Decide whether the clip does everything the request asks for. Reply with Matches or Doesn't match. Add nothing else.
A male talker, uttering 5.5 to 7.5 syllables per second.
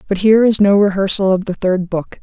Doesn't match